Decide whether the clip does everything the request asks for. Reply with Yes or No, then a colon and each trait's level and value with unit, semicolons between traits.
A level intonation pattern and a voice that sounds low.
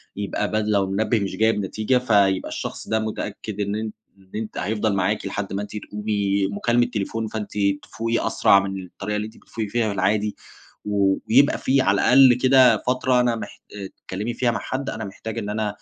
Yes: narrow, 2.3 semitones; low, 105 Hz